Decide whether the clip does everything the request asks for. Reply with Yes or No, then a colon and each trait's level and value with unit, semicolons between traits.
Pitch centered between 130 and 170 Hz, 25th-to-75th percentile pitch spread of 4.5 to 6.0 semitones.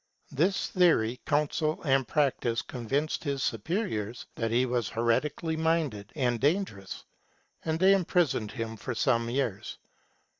Yes: low, 135 Hz; wide, 5.6 semitones